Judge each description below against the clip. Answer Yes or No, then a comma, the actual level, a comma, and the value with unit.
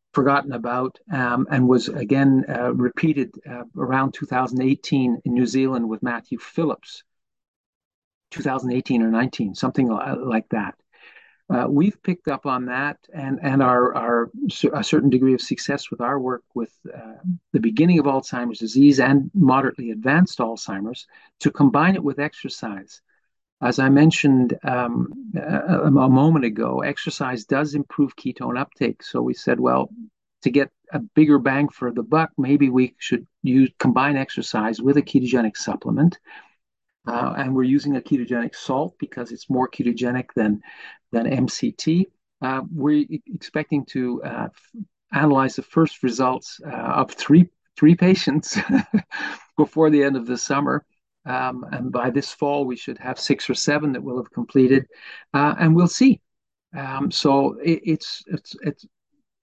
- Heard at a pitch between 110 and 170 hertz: Yes, medium, 140 Hz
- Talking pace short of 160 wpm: Yes, average, 150 wpm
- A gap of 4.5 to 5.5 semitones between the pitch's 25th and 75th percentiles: No, average, 3.3 semitones